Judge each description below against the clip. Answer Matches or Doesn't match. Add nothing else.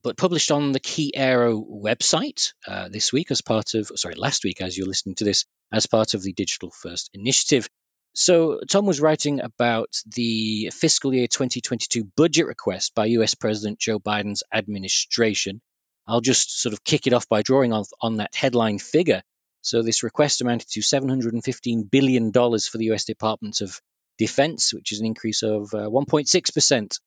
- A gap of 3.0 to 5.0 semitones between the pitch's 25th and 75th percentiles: Matches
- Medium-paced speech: Matches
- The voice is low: Matches